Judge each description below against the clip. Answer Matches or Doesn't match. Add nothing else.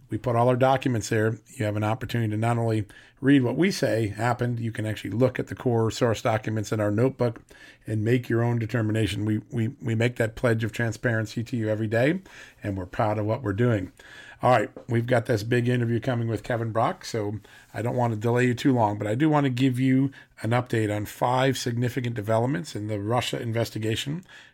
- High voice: Doesn't match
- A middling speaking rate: Doesn't match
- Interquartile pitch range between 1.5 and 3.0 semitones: Matches